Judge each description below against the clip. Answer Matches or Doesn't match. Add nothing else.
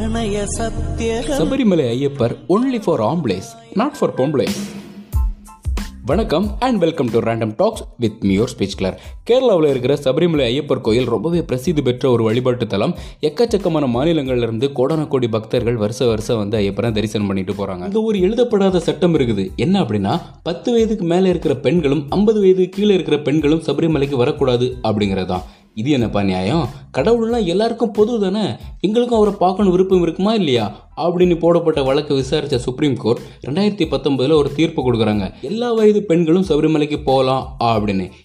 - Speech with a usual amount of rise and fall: Doesn't match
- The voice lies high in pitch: Doesn't match